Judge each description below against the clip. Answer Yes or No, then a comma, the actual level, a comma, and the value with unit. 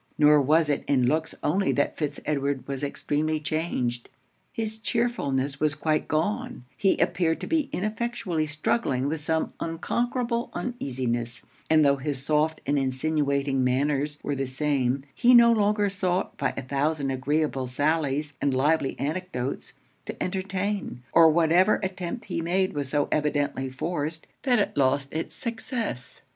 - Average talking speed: Yes, average, 150 wpm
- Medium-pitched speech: Yes, medium, 150 Hz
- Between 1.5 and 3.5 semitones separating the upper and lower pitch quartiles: No, average, 5.0 semitones